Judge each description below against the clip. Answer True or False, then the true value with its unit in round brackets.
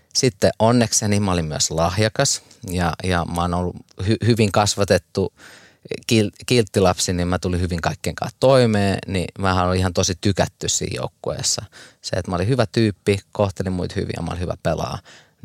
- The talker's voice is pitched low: True (95 Hz)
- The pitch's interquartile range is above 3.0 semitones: True (3.4 semitones)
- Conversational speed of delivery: False (175 wpm)